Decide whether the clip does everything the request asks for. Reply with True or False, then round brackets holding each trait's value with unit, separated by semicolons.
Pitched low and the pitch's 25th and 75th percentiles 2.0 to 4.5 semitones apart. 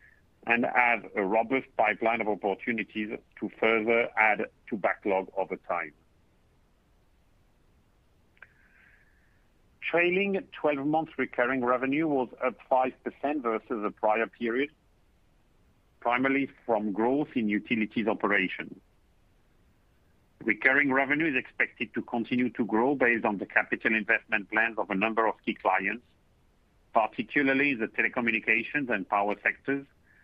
False (115 Hz; 4.9 semitones)